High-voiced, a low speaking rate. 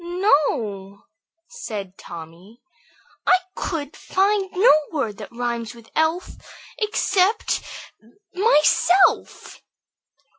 Yes: very high, 300 Hz; slow, 80 wpm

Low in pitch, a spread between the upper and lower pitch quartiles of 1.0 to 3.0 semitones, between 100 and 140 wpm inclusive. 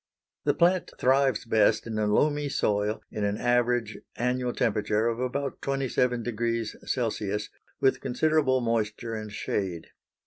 No: low, 120 Hz; average, 3.4 semitones; slow, 135 wpm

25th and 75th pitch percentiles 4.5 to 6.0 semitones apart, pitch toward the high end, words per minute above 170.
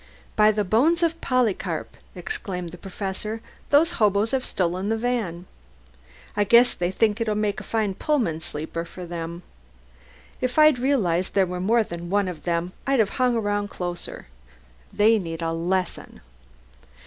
No: average, 4.8 semitones; high, 205 Hz; average, 160 wpm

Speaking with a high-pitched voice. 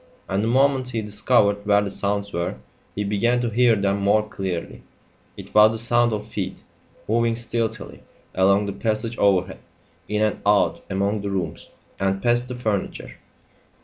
No: low, 105 Hz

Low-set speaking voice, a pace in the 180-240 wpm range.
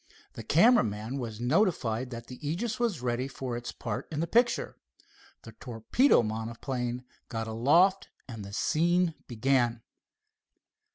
No: low, 125 Hz; slow, 135 wpm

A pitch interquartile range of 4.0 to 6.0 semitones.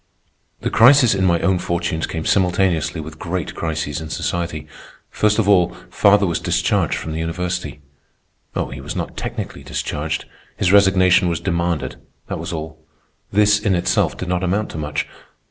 No: average, 3.2 semitones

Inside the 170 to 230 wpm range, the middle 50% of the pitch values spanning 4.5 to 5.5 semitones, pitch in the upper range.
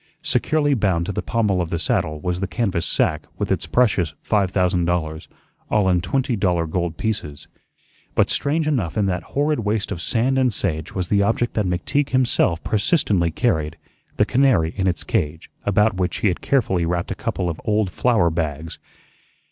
No: average, 185 wpm; average, 5.2 semitones; very low, 95 Hz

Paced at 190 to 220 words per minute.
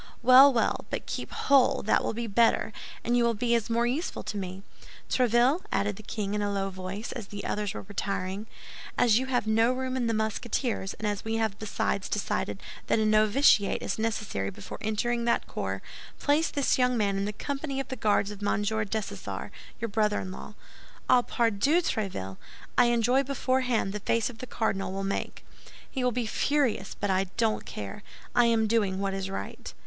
Yes: average, 195 wpm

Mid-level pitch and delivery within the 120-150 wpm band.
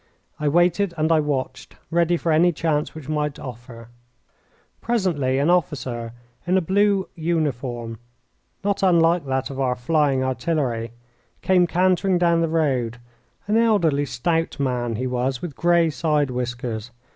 Yes: medium, 150 Hz; average, 145 wpm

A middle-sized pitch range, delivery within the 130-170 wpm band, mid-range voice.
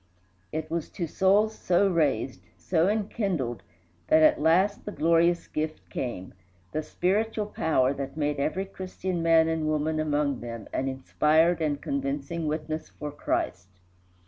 Yes: average, 3.4 semitones; average, 145 wpm; medium, 160 Hz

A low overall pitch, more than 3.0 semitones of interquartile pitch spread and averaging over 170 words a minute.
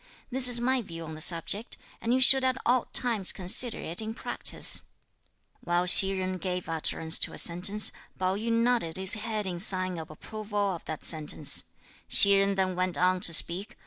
No: high, 190 Hz; average, 4.1 semitones; average, 190 wpm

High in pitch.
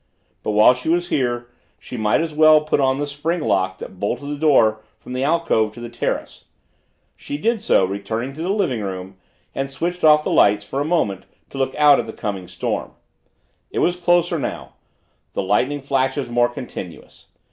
No: low, 135 Hz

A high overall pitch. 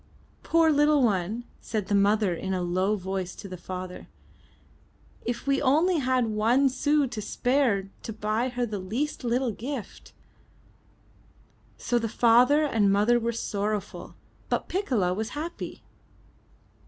Yes: high, 230 Hz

